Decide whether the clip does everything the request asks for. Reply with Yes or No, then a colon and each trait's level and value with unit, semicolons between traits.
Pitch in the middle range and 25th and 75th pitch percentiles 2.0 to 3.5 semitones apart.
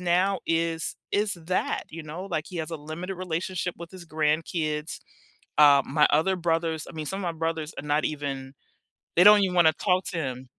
Yes: medium, 165 Hz; average, 2.8 semitones